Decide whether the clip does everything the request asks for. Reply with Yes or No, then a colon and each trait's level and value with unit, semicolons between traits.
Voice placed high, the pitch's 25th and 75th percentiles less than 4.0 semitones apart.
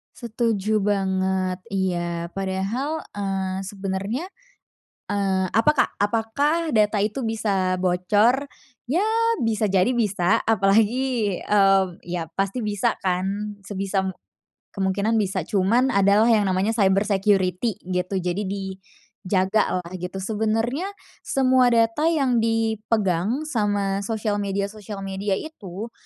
Yes: high, 205 Hz; average, 2.9 semitones